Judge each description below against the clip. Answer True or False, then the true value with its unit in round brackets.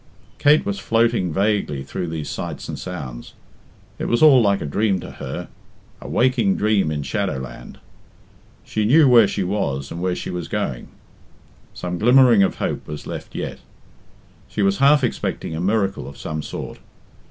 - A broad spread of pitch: True (6.1 semitones)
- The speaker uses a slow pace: False (170 wpm)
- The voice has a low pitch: True (100 Hz)